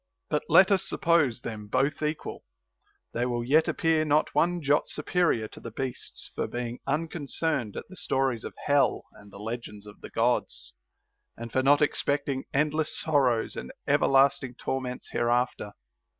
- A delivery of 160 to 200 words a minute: Yes, average, 165 wpm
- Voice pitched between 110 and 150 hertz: Yes, low, 135 Hz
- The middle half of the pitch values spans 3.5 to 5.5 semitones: Yes, average, 4.3 semitones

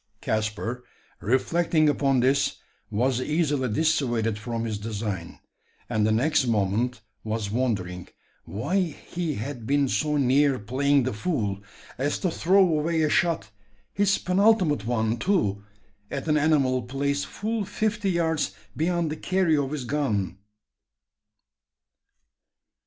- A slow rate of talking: Yes, slow, 125 wpm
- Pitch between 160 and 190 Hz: No, low, 135 Hz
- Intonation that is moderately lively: No, wide, 6.1 semitones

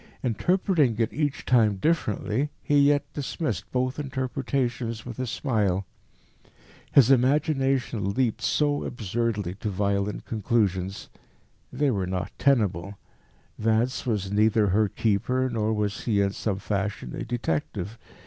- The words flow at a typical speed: No, slow, 125 wpm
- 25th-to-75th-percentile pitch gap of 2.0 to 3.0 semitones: No, average, 4.5 semitones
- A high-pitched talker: No, low, 115 Hz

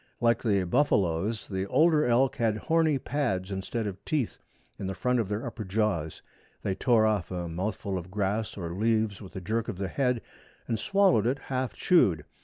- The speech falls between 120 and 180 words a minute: No, average, 190 wpm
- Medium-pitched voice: No, low, 110 Hz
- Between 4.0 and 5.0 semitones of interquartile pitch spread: Yes, average, 4.4 semitones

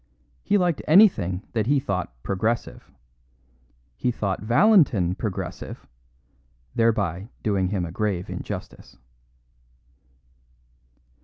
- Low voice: Yes, low, 105 Hz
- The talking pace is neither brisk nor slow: No, slow, 90 wpm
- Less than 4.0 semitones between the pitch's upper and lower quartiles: No, average, 5.2 semitones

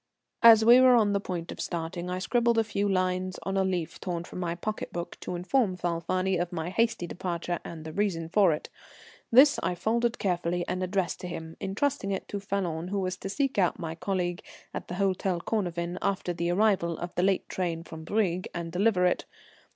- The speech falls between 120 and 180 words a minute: No, fast, 205 wpm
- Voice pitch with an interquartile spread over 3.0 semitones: No, narrow, 2.6 semitones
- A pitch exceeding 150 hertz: Yes, medium, 185 Hz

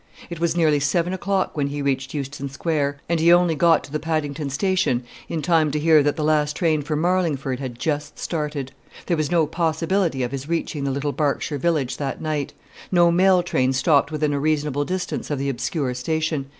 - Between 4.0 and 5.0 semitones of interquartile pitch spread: No, average, 2.9 semitones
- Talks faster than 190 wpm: Yes, average, 200 wpm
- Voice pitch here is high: No, medium, 150 Hz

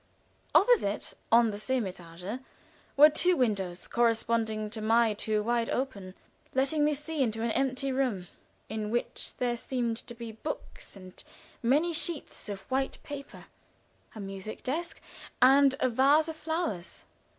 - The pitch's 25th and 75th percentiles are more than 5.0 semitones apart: No, average, 4.3 semitones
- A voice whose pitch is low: No, high, 240 Hz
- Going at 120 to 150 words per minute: Yes, average, 145 wpm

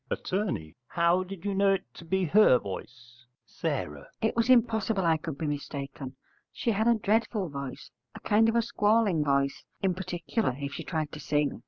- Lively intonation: Yes, wide, 6.8 semitones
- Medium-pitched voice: Yes, medium, 175 Hz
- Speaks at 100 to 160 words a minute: No, average, 185 wpm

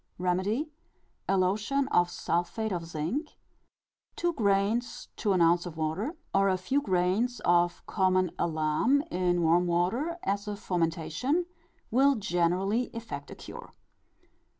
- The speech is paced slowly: Yes, slow, 130 wpm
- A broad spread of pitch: No, average, 4.9 semitones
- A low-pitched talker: No, high, 190 Hz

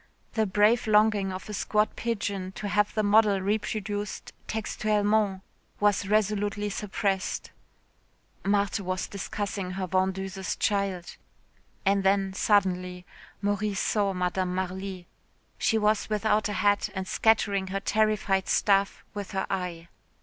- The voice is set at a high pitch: Yes, high, 200 Hz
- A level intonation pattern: Yes, narrow, 1.7 semitones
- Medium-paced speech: No, slow, 125 wpm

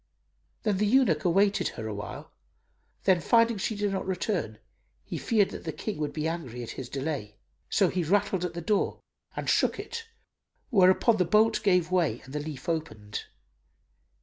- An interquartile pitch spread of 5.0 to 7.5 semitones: Yes, wide, 5.6 semitones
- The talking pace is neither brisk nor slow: Yes, average, 175 wpm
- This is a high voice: No, medium, 180 Hz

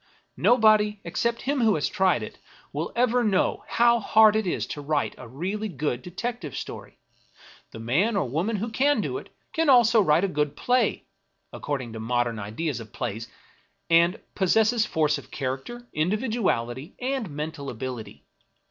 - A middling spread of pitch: No, wide, 8.4 semitones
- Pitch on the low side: No, medium, 180 Hz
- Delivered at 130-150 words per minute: No, average, 165 wpm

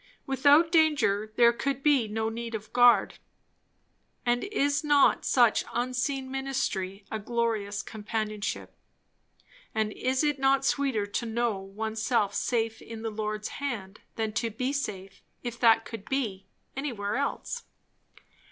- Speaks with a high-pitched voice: Yes, high, 235 Hz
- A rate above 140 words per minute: No, slow, 135 wpm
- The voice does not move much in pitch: No, average, 4.0 semitones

